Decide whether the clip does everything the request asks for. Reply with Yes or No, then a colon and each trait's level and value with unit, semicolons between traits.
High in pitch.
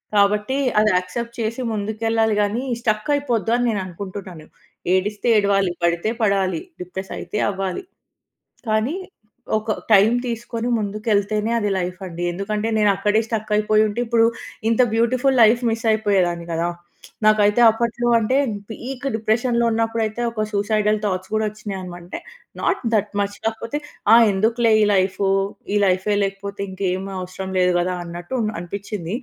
Yes: high, 210 Hz